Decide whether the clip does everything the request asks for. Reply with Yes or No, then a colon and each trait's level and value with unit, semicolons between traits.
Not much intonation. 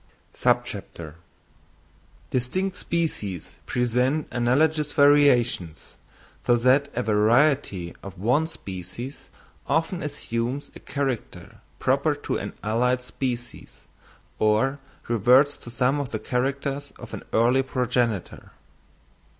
No: average, 3.6 semitones